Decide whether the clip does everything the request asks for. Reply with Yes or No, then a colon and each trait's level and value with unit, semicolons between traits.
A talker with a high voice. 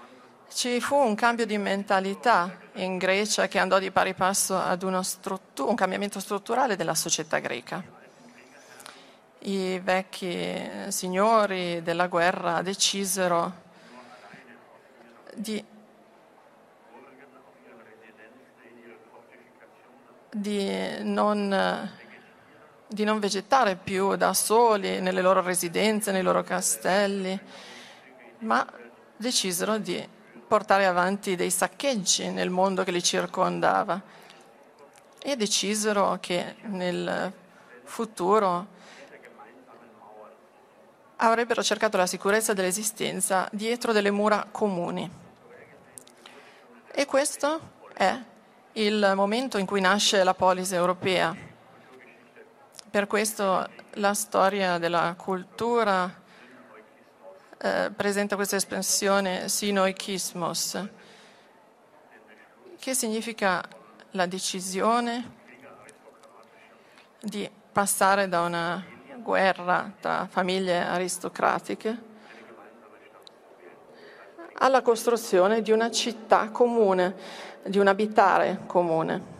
Yes: high, 195 Hz